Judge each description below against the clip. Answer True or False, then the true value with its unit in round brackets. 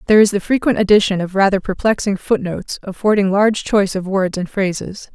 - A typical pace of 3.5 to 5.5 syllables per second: False (6.1 syllables/s)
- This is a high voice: True (200 Hz)